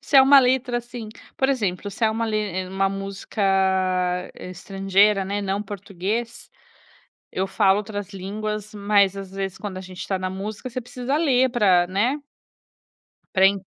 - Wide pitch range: No, average, 3.2 semitones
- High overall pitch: Yes, high, 205 Hz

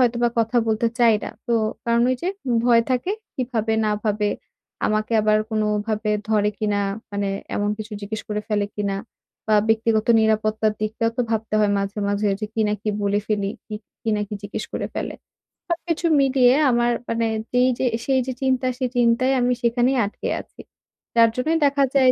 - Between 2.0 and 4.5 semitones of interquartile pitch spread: Yes, average, 2.7 semitones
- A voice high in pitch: Yes, high, 225 Hz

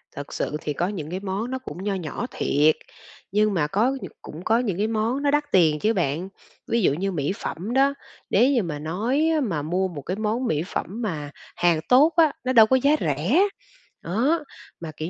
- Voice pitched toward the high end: Yes, high, 195 Hz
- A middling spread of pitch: No, wide, 7.2 semitones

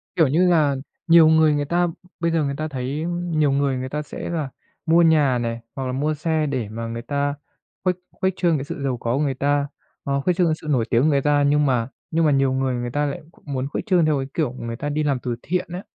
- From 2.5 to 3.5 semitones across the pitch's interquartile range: Yes, average, 3.2 semitones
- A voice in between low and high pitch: Yes, medium, 145 Hz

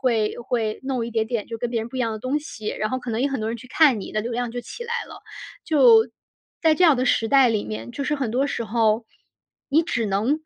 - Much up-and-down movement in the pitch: No, average, 3.4 semitones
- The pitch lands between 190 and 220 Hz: No, high, 240 Hz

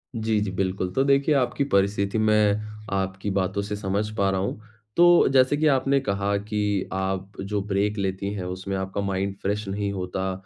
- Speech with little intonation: Yes, narrow, 1.8 semitones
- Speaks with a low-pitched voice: Yes, low, 100 Hz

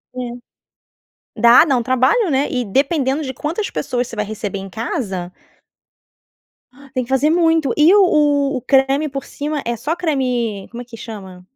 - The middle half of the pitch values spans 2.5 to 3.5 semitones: No, average, 4.1 semitones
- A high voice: Yes, very high, 260 Hz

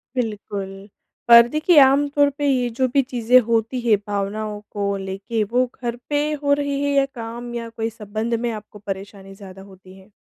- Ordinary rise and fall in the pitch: Yes, average, 4.0 semitones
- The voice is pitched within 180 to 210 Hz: No, high, 230 Hz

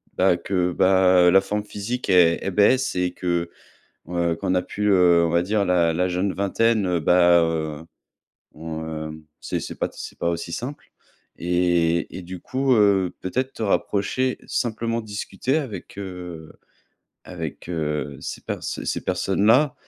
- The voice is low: Yes, very low, 90 Hz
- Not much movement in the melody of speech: No, average, 3.3 semitones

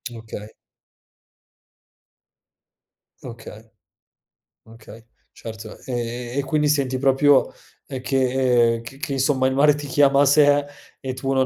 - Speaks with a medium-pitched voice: No, low, 130 Hz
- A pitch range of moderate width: Yes, average, 3.1 semitones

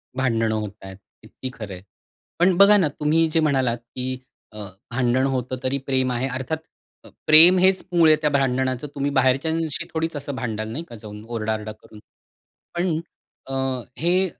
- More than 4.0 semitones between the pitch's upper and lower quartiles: Yes, average, 5.2 semitones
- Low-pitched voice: Yes, low, 130 Hz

